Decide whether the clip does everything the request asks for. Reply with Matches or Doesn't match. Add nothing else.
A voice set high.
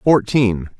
Doesn't match